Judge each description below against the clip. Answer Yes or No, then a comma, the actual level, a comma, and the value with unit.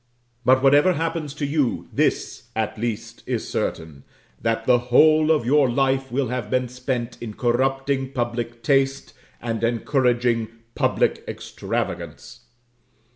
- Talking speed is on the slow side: Yes, slow, 130 wpm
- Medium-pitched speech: No, low, 125 Hz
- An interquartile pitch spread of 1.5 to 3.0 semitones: Yes, narrow, 2.6 semitones